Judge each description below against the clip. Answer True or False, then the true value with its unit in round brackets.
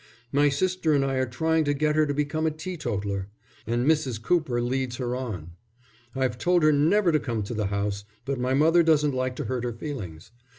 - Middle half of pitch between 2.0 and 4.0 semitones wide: False (4.4 semitones)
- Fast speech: True (210 wpm)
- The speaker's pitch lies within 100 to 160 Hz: True (135 Hz)